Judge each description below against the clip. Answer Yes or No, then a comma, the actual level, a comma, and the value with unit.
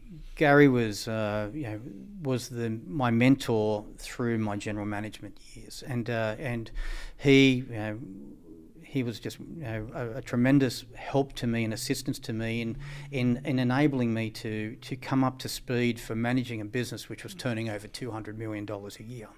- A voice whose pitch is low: Yes, low, 120 Hz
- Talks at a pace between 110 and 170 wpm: No, average, 180 wpm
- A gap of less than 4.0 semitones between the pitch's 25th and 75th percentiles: Yes, average, 3.3 semitones